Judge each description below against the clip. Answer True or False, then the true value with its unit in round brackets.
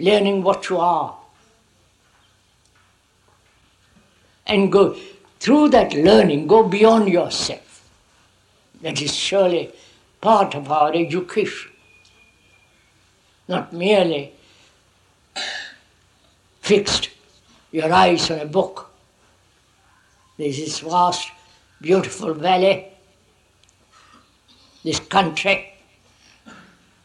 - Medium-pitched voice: True (160 Hz)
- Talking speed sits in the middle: False (75 wpm)